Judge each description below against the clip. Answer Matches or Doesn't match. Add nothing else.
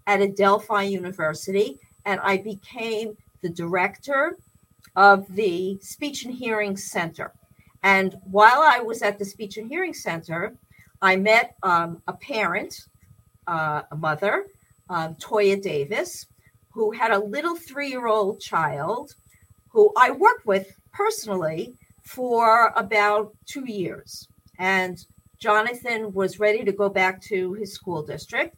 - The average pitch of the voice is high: Matches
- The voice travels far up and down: Doesn't match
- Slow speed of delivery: Matches